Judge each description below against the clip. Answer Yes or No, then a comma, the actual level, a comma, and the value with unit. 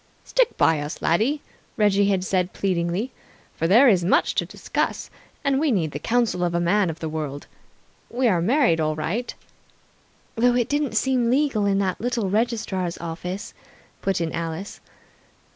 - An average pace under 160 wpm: No, average, 170 wpm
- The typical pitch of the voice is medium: No, high, 195 Hz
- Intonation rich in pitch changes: Yes, wide, 6.0 semitones